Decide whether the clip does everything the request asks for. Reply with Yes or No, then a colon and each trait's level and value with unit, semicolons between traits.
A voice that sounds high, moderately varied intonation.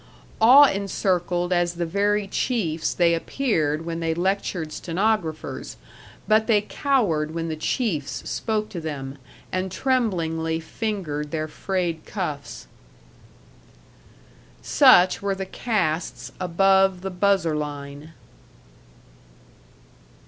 No: medium, 175 Hz; average, 3.9 semitones